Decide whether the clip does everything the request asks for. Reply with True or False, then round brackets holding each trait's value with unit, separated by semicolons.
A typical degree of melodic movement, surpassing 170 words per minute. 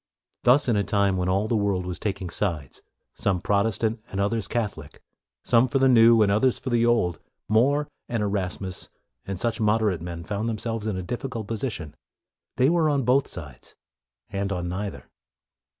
True (3.8 semitones; 180 wpm)